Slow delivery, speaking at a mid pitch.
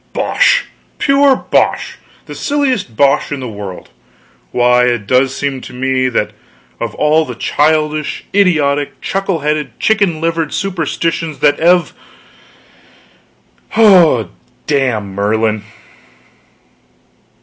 Yes: slow, 105 wpm; medium, 145 Hz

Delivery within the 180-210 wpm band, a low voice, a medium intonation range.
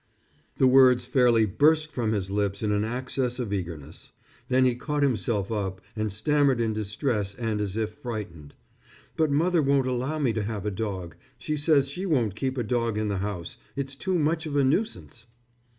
Yes: average, 190 wpm; low, 120 Hz; average, 5.0 semitones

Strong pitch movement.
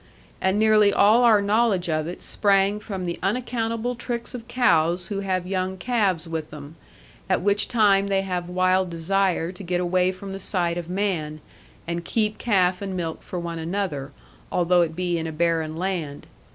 No: average, 3.0 semitones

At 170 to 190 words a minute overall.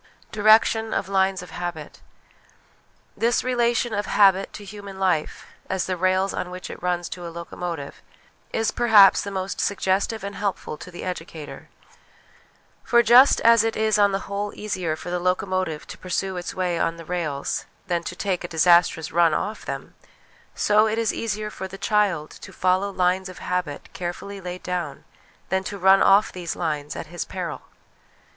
Yes: average, 175 wpm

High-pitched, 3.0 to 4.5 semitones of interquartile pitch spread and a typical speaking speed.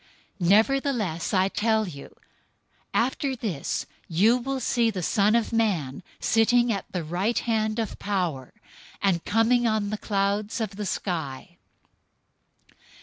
No: high, 210 Hz; average, 3.9 semitones; slow, 130 wpm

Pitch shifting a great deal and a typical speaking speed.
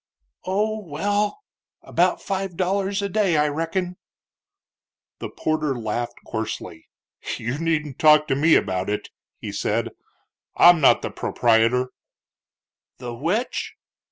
No: wide, 7.9 semitones; slow, 120 wpm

